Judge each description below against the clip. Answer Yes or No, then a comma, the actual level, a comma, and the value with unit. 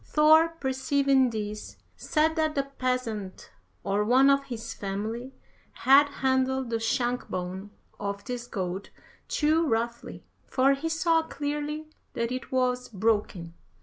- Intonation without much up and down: No, average, 4.2 semitones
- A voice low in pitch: No, very high, 255 Hz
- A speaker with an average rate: No, slow, 130 wpm